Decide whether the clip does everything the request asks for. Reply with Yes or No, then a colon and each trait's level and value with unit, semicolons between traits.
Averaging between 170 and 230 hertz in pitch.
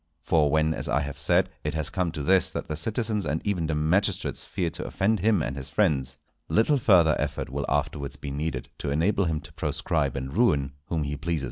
No: very low, 80 Hz